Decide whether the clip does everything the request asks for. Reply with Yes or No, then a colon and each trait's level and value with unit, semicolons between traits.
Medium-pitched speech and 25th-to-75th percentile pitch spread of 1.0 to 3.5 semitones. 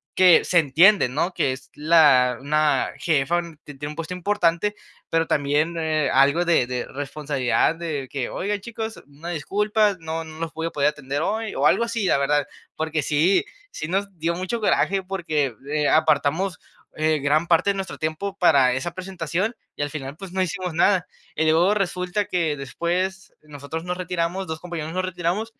No: medium, 165 Hz; average, 3.9 semitones